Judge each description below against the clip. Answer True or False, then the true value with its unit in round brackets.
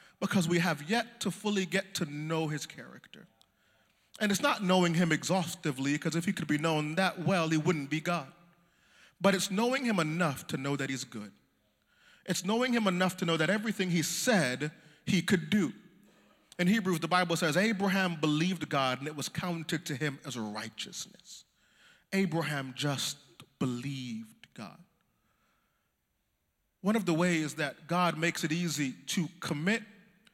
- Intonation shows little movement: False (4.1 semitones)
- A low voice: False (170 Hz)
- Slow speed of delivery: False (165 wpm)